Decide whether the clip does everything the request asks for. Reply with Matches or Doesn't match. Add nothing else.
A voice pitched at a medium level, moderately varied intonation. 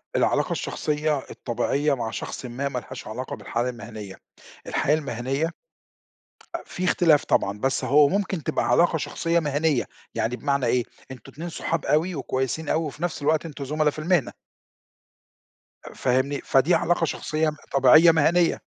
Matches